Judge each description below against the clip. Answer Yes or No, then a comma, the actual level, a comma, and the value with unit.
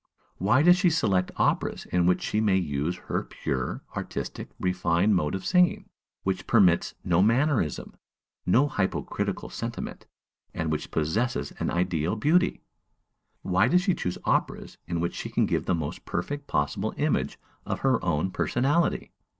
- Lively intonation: Yes, wide, 7.3 semitones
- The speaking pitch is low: Yes, very low, 95 Hz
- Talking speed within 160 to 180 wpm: No, average, 150 wpm